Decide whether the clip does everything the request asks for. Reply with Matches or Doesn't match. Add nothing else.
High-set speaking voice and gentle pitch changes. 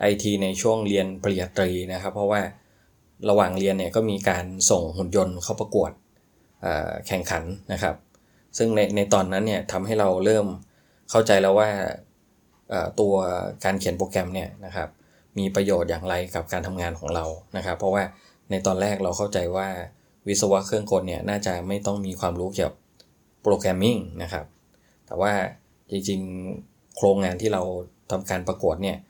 Doesn't match